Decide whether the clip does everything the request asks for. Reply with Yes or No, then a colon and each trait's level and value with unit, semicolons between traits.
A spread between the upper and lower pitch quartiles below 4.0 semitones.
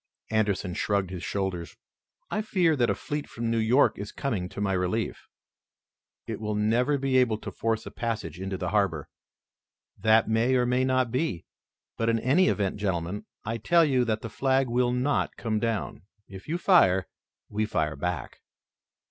No: average, 4.5 semitones